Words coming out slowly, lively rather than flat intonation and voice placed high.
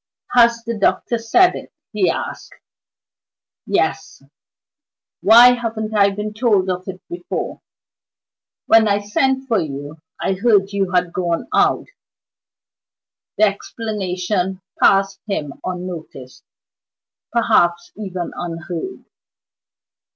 No: slow, 110 wpm; average, 3.8 semitones; high, 195 Hz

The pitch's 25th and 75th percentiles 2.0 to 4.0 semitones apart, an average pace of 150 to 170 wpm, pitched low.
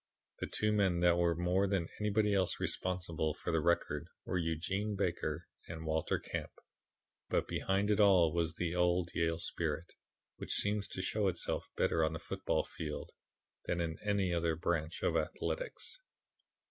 Yes: average, 3.0 semitones; average, 160 wpm; very low, 85 Hz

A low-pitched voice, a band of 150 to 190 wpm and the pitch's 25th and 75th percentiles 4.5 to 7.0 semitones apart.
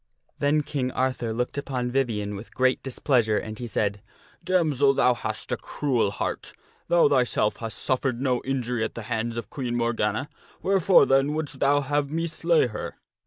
No: low, 130 Hz; average, 175 wpm; average, 3.5 semitones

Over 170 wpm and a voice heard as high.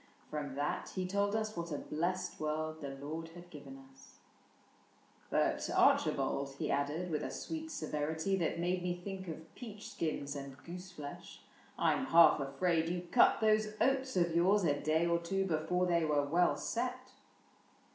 No: average, 180 wpm; medium, 170 Hz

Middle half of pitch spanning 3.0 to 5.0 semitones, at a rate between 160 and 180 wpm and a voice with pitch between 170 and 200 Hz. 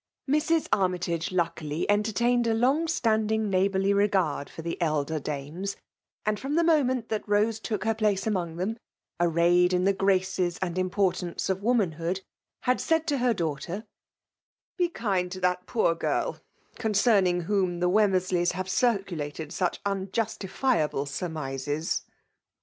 No: average, 4.1 semitones; average, 145 wpm; high, 190 Hz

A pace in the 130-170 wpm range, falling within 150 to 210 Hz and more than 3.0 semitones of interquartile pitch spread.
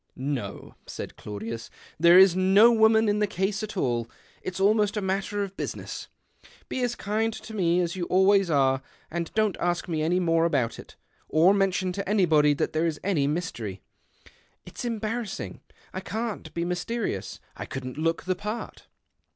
No: average, 180 wpm; medium, 185 Hz; average, 4.5 semitones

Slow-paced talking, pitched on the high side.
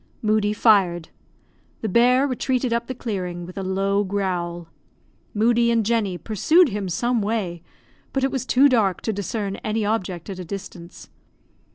No: average, 160 wpm; high, 210 Hz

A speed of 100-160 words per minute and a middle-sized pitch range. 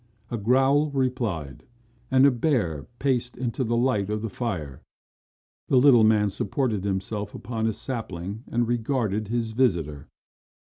Yes: average, 140 wpm; average, 4.1 semitones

